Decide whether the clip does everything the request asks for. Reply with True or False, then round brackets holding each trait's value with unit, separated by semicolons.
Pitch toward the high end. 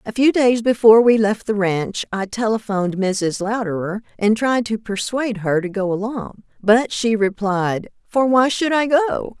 True (220 Hz)